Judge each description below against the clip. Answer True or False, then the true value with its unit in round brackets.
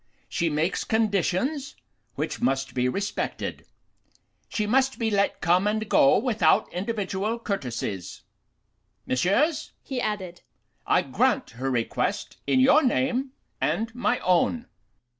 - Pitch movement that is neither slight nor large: False (6.3 semitones)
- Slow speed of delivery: True (120 wpm)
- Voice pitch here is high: True (210 Hz)